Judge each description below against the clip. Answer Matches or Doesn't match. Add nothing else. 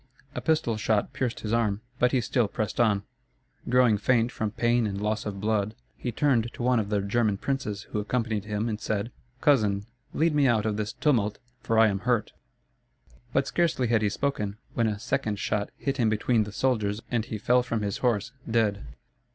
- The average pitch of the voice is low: Matches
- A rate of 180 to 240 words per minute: Matches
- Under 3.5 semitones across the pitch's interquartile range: Matches